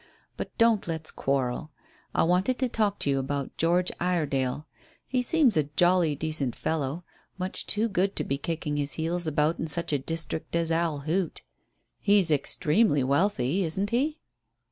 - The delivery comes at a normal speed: Yes, average, 165 wpm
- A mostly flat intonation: No, average, 4.6 semitones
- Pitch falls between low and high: Yes, medium, 165 Hz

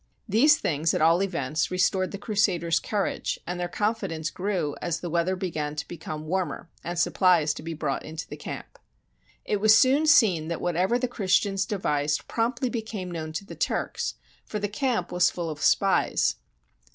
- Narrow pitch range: No, average, 4.3 semitones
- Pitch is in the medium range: Yes, medium, 180 Hz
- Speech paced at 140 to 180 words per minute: No, average, 190 wpm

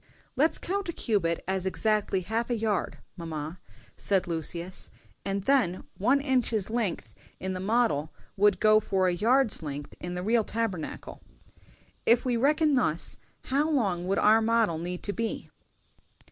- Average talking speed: Yes, average, 155 wpm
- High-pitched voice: Yes, high, 205 Hz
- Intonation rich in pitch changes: No, average, 4.8 semitones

